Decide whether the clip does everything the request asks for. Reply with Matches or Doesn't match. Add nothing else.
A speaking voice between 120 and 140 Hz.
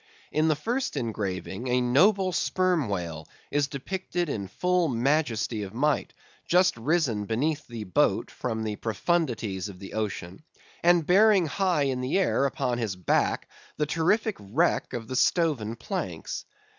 Matches